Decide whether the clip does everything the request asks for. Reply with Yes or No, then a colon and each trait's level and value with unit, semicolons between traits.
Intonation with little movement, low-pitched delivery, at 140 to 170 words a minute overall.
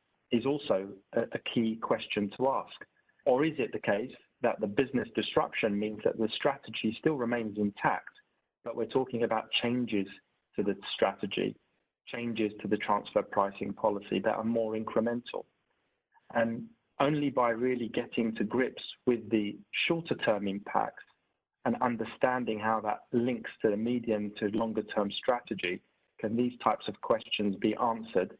Yes: narrow, 2.2 semitones; low, 115 Hz; average, 150 wpm